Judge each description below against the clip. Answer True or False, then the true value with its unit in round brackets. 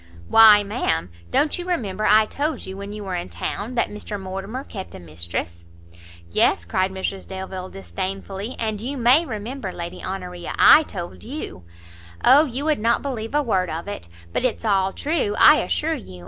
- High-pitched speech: True (200 Hz)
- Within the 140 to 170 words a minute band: False (190 wpm)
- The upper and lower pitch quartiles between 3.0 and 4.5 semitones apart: False (5.5 semitones)